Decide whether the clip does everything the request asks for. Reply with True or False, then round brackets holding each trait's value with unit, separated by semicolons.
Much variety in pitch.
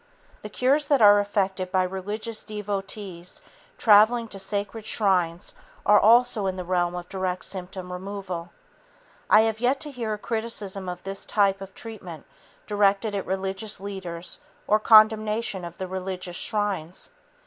False (2.6 semitones)